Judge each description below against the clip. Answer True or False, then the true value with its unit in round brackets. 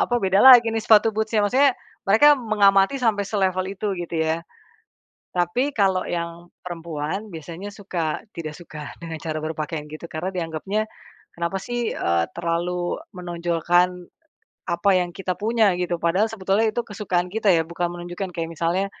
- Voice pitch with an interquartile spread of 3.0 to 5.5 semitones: True (3.8 semitones)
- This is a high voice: False (180 Hz)